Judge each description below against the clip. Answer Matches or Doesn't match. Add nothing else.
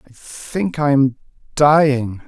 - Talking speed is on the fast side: Doesn't match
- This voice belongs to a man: Matches